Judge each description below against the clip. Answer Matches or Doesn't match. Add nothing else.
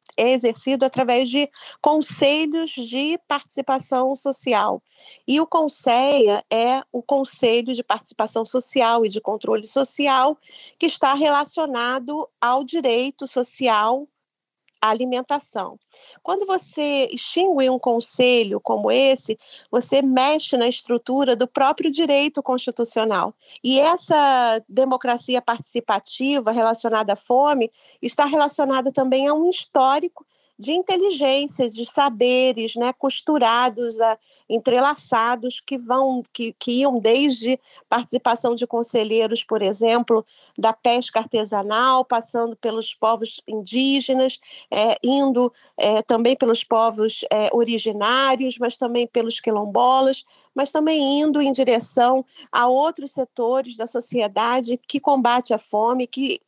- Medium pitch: Doesn't match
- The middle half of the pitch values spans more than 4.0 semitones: Doesn't match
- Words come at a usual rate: Doesn't match